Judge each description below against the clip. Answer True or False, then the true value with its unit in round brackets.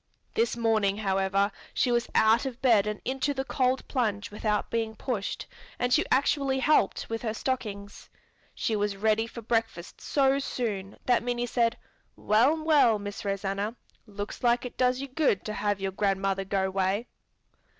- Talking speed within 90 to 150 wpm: False (165 wpm)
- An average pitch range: True (3.7 semitones)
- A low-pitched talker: False (225 Hz)